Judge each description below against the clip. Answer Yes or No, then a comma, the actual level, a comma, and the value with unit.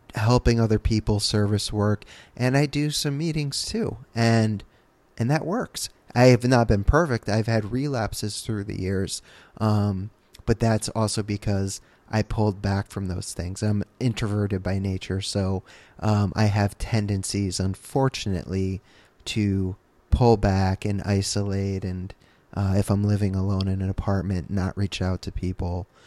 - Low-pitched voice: Yes, low, 105 Hz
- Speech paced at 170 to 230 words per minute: No, average, 150 wpm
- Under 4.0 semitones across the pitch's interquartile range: Yes, average, 2.7 semitones